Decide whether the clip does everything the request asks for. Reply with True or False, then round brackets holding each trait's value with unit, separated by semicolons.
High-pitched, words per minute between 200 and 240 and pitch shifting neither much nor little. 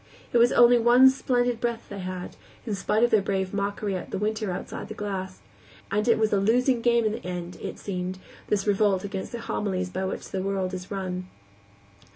True (200 Hz; 205 wpm; 3.5 semitones)